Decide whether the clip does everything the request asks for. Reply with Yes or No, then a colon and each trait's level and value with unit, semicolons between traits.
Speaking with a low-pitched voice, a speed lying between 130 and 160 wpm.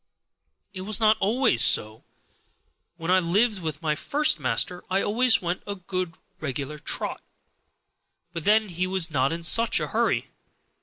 No: medium, 180 Hz; average, 155 wpm